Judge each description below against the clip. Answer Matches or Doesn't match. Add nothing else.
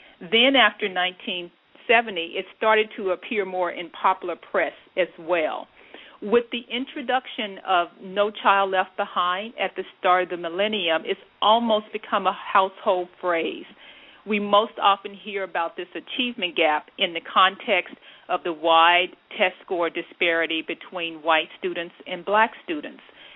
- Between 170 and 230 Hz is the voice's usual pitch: Matches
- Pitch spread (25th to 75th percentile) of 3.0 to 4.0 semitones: Matches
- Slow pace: Doesn't match